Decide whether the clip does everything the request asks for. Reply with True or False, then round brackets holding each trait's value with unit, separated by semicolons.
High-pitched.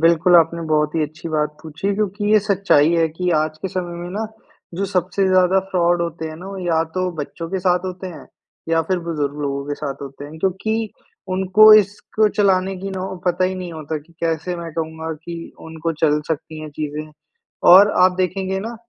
False (170 Hz)